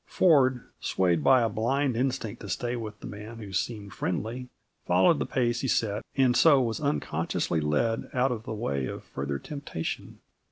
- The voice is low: Yes, low, 115 Hz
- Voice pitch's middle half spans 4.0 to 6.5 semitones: Yes, average, 4.3 semitones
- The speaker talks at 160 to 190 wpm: Yes, average, 175 wpm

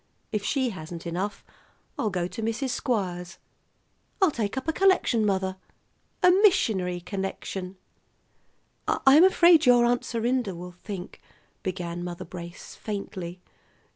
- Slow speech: Yes, slow, 130 wpm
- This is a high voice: Yes, high, 200 Hz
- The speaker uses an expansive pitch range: Yes, wide, 5.7 semitones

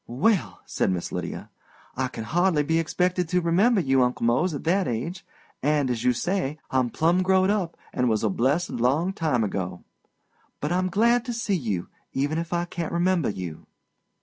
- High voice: No, medium, 160 Hz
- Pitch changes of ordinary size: No, wide, 6.5 semitones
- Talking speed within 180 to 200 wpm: Yes, average, 185 wpm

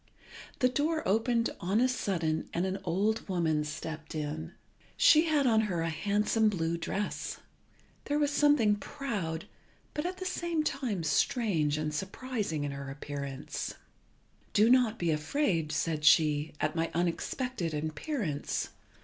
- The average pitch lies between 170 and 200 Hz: Yes, high, 190 Hz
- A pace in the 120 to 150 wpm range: Yes, average, 140 wpm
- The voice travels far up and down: Yes, wide, 8.1 semitones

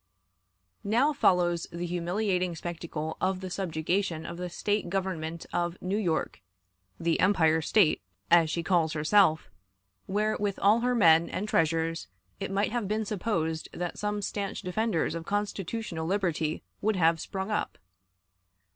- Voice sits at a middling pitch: Yes, medium, 180 Hz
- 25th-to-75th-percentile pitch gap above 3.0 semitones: Yes, average, 3.7 semitones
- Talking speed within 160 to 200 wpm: No, average, 145 wpm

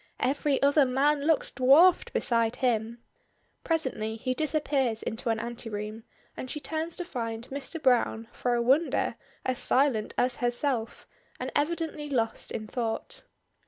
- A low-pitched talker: No, very high, 255 Hz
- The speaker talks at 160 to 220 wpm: No, average, 140 wpm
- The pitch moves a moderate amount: Yes, average, 4.3 semitones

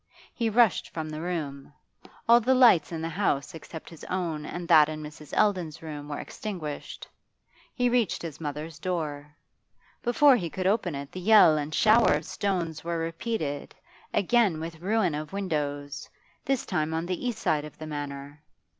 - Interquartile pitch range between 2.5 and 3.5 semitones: No, average, 4.9 semitones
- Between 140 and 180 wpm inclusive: Yes, average, 175 wpm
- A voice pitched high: No, medium, 165 Hz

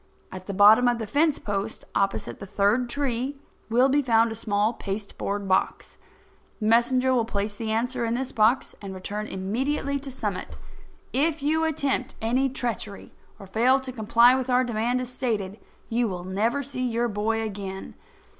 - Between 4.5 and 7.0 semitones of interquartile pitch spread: No, average, 3.8 semitones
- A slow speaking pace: No, average, 175 wpm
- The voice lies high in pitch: Yes, high, 230 Hz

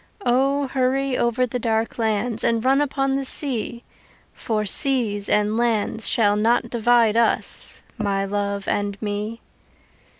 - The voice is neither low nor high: No, high, 230 Hz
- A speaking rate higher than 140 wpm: No, slow, 135 wpm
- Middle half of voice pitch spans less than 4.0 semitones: Yes, average, 3.2 semitones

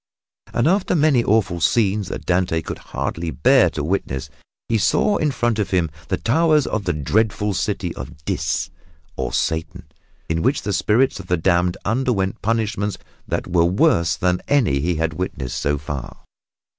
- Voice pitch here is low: Yes, very low, 95 Hz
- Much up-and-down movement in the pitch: Yes, wide, 6.0 semitones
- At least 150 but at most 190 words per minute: Yes, average, 170 wpm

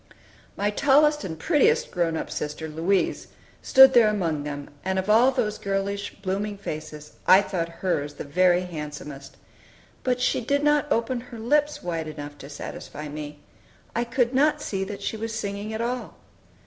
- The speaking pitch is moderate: No, high, 200 Hz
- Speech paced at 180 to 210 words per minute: No, average, 170 wpm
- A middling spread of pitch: No, wide, 7.4 semitones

